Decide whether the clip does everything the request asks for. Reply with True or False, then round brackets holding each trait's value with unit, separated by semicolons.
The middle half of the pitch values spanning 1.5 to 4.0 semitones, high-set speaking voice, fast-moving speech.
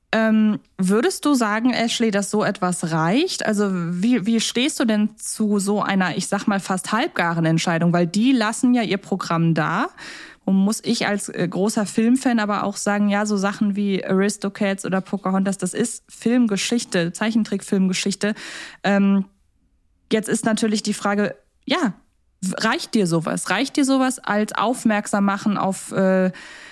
False (2.8 semitones; 210 Hz; 155 wpm)